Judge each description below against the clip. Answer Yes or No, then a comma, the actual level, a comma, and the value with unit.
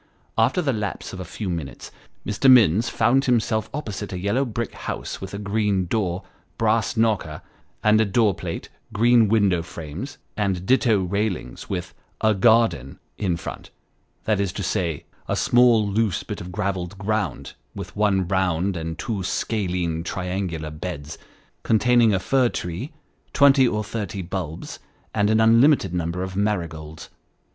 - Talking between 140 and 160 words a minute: Yes, average, 155 wpm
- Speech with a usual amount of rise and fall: Yes, average, 3.9 semitones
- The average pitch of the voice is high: No, low, 100 Hz